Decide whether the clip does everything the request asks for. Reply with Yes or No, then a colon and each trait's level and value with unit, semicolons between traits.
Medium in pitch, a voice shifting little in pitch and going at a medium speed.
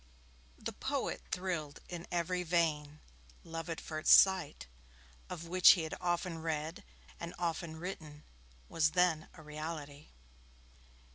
No: medium, 165 Hz; narrow, 2.2 semitones; slow, 125 wpm